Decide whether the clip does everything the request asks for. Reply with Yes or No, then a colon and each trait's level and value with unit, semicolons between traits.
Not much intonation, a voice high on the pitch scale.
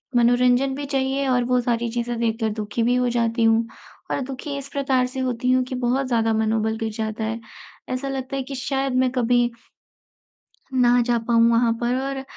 Yes: narrow, 2.3 semitones; high, 245 Hz